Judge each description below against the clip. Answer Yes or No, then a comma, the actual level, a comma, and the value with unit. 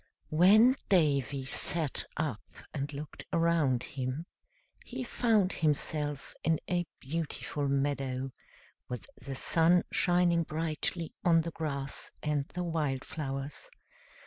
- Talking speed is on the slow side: Yes, slow, 115 wpm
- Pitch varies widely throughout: No, average, 3.5 semitones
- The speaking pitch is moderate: Yes, medium, 155 Hz